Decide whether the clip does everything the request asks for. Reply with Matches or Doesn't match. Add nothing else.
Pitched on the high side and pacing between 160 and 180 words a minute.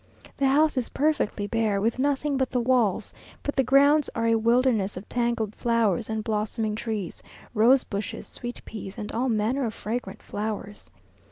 Matches